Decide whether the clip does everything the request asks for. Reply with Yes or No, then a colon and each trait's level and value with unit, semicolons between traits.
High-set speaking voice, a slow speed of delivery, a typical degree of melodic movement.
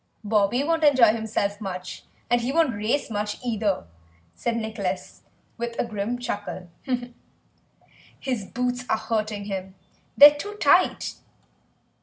Yes: high, 220 Hz; slow, 125 wpm; average, 3.3 semitones